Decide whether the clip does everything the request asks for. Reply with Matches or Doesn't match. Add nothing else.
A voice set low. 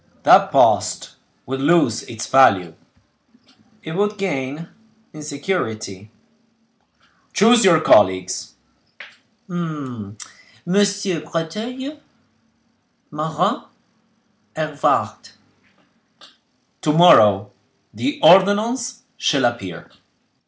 Doesn't match